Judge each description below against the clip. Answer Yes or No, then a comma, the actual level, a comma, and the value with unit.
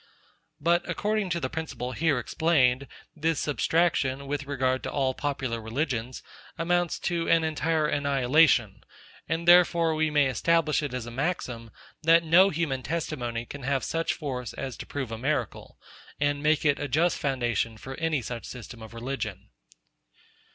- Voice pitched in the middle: Yes, medium, 145 Hz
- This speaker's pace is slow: No, average, 160 wpm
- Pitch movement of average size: Yes, average, 4.5 semitones